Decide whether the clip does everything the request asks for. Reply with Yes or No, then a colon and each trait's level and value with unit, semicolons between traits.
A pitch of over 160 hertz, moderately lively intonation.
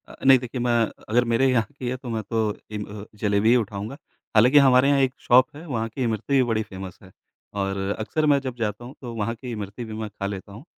No: low, 115 Hz; average, 3.3 semitones